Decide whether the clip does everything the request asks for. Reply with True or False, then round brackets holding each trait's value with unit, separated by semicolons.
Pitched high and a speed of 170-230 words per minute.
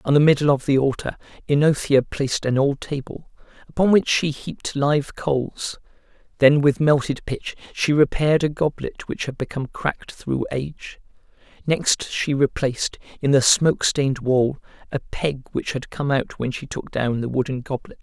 False (140 Hz; 175 wpm)